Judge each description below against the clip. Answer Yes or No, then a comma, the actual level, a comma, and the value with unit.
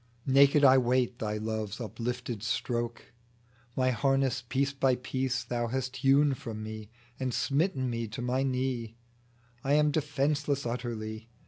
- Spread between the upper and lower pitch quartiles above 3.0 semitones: No, narrow, 2.6 semitones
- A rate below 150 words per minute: Yes, average, 140 wpm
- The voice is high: No, low, 125 Hz